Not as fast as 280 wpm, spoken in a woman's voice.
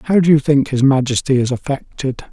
No: fast, 205 wpm; male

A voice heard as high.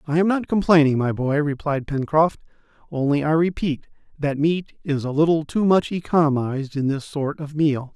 No: medium, 150 Hz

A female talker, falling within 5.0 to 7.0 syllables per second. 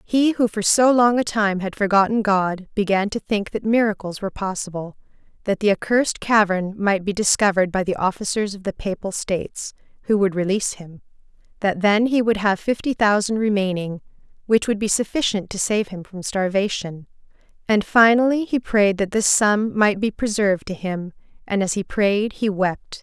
Yes: female; 5.1 syllables/s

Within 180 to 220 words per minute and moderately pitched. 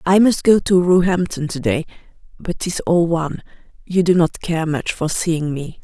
Yes: average, 195 wpm; medium, 170 Hz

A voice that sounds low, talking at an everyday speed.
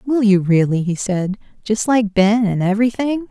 No: high, 210 Hz; average, 165 wpm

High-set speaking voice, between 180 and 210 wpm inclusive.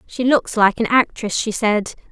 Yes: high, 225 Hz; average, 200 wpm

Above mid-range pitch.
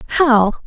Yes: very high, 250 Hz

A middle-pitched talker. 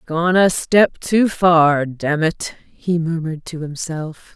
Yes: medium, 165 Hz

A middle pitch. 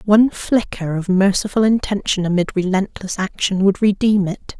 No: high, 195 Hz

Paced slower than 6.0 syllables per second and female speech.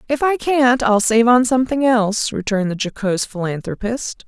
Yes: 5.5 syllables/s; female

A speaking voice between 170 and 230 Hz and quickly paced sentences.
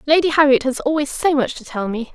No: very high, 275 Hz; fast, 250 wpm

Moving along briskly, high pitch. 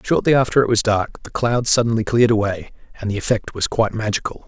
No: fast, 215 wpm; low, 110 Hz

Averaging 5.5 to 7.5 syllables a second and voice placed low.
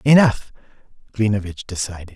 Yes: 5.6 syllables/s; low, 105 Hz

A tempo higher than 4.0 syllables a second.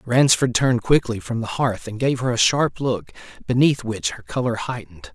Yes: 5.1 syllables/s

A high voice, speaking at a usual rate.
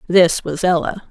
No: medium, 175 Hz; average, 165 wpm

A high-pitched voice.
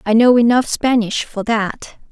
Yes: high, 230 Hz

